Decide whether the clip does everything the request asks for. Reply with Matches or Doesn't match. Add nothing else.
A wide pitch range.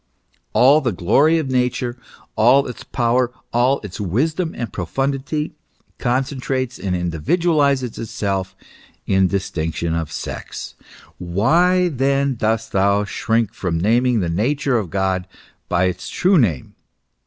Matches